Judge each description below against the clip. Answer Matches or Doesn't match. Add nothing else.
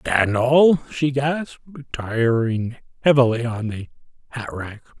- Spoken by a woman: Doesn't match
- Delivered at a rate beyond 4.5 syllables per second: Doesn't match